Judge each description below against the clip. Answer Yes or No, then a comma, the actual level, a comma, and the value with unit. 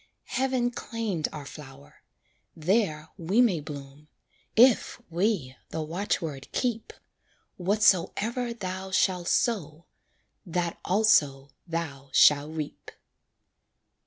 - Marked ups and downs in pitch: Yes, wide, 6.2 semitones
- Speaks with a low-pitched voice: No, medium, 175 Hz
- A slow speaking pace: Yes, slow, 95 wpm